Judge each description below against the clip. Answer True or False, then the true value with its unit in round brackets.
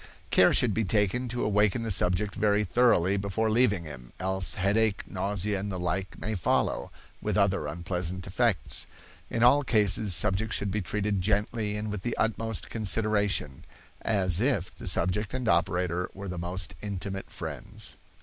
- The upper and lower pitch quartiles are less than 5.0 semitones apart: True (2.8 semitones)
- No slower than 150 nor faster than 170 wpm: True (160 wpm)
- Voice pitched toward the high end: False (100 Hz)